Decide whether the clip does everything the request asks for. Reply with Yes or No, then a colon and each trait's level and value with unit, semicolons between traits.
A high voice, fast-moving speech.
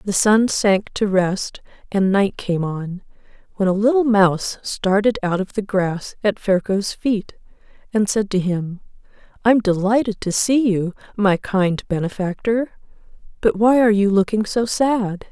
No: high, 205 Hz; average, 155 wpm